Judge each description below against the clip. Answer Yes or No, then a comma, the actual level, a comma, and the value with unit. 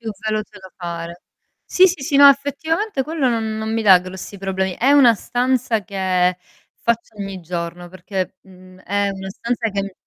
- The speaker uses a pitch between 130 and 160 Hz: No, high, 200 Hz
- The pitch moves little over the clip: No, average, 4.7 semitones